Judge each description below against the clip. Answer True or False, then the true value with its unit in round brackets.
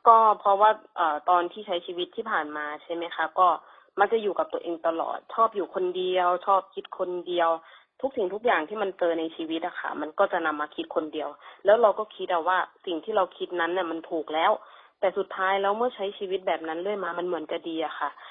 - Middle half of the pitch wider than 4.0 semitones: False (3.2 semitones)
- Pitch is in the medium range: True (180 Hz)